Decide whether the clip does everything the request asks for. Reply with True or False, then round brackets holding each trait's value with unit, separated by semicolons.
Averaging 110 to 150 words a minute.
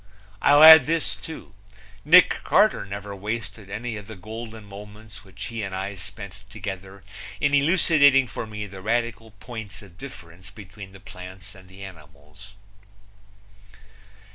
True (140 wpm)